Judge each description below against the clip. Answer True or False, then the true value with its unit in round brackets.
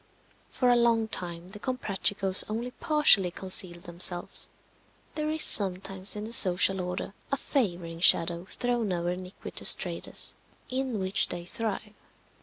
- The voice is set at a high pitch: True (195 Hz)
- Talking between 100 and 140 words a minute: True (135 wpm)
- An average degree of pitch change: True (4.7 semitones)